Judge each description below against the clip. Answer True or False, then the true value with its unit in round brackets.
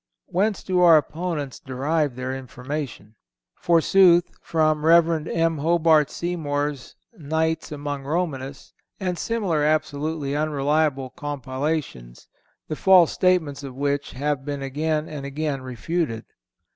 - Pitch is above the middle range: False (150 Hz)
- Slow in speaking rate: True (115 wpm)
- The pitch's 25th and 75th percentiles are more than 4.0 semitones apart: False (3.0 semitones)